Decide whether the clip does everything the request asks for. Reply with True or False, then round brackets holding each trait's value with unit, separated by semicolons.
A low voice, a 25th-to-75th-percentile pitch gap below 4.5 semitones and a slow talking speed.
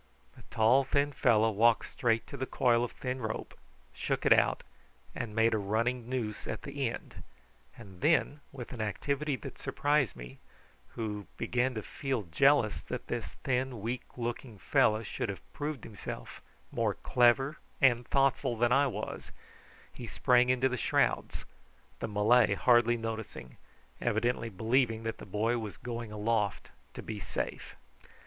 False (120 Hz; 2.9 semitones; 155 wpm)